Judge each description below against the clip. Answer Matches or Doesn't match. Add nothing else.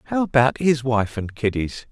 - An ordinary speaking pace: Matches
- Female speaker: Doesn't match